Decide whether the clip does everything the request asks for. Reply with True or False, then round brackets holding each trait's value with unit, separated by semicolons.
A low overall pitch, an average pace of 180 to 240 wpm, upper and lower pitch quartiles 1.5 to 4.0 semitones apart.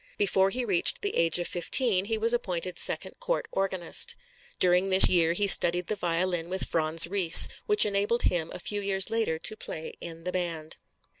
False (185 Hz; 190 wpm; 3.3 semitones)